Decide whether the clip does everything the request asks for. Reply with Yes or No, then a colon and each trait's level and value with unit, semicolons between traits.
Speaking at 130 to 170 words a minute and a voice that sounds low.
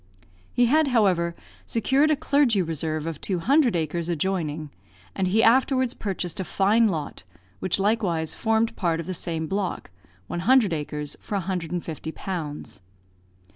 No: average, 145 wpm; medium, 185 Hz